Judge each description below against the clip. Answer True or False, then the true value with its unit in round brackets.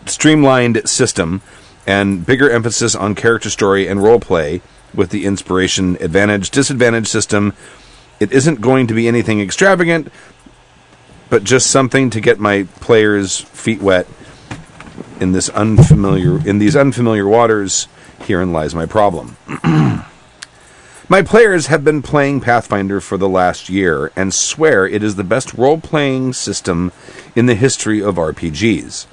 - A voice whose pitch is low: True (110 Hz)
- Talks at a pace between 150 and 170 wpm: False (140 wpm)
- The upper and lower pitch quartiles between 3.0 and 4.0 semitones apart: False (5.0 semitones)